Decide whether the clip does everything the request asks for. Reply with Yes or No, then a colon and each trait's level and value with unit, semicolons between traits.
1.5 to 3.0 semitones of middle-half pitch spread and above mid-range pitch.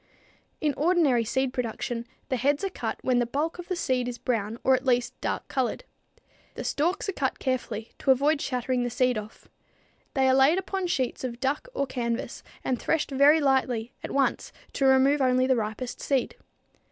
Yes: average, 2.7 semitones; very high, 260 Hz